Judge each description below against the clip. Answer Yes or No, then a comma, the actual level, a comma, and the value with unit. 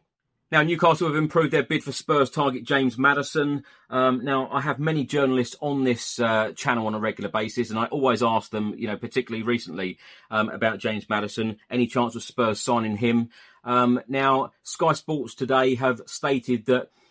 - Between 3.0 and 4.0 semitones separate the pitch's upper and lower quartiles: Yes, average, 3.3 semitones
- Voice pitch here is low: Yes, low, 125 Hz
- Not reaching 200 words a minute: Yes, average, 180 wpm